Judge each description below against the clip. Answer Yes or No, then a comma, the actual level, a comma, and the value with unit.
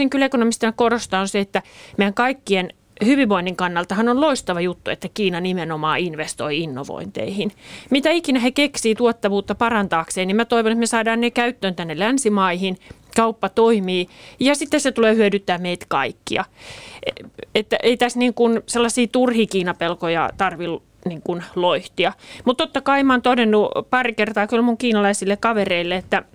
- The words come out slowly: No, fast, 155 wpm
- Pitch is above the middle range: Yes, high, 215 Hz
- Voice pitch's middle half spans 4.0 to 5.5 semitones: Yes, average, 4.6 semitones